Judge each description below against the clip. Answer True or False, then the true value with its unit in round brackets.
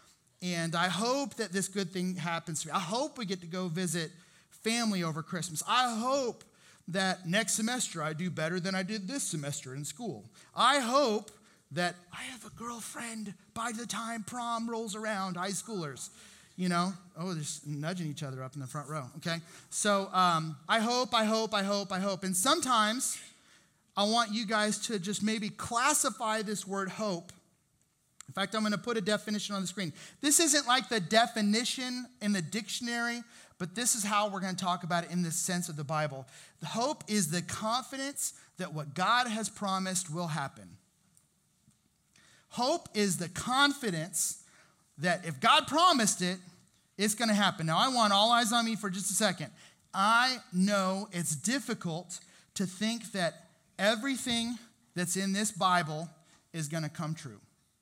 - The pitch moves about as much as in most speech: True (4.7 semitones)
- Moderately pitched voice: False (195 Hz)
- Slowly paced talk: False (180 wpm)